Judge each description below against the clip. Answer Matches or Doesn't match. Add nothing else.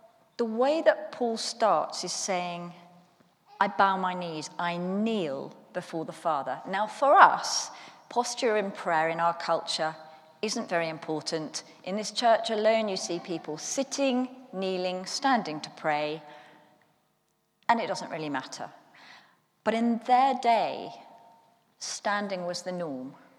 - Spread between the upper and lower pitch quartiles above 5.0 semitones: Matches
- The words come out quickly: Doesn't match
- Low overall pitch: Doesn't match